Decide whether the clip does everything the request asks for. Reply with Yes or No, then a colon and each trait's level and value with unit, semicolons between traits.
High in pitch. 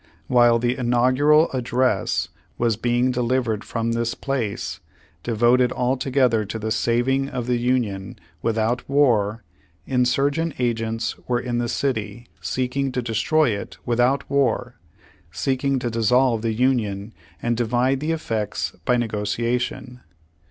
No: low, 120 Hz